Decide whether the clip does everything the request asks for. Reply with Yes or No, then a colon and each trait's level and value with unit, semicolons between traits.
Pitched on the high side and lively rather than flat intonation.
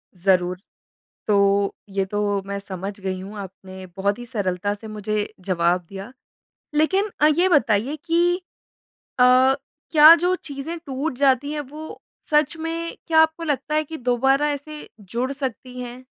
Yes: very high, 250 Hz; wide, 7.2 semitones